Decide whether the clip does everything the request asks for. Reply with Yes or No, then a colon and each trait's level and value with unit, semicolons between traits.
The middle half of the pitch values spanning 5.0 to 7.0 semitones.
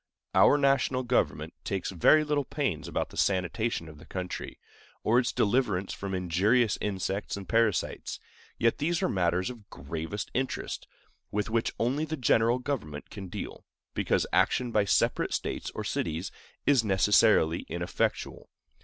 Yes: wide, 5.6 semitones